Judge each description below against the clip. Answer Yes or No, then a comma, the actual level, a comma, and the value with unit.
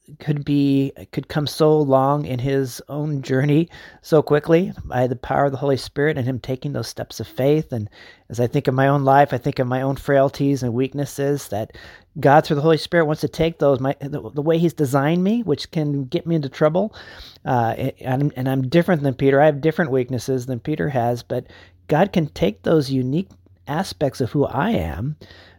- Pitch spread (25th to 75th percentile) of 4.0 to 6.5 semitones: No, average, 2.7 semitones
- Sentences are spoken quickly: Yes, fast, 210 wpm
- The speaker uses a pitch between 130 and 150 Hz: Yes, medium, 140 Hz